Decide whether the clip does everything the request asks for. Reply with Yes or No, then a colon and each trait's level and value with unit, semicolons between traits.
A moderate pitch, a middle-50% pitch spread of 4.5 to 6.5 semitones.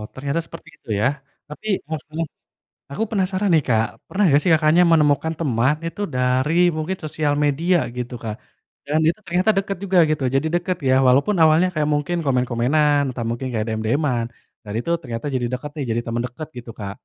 Yes: medium, 145 Hz; average, 4.9 semitones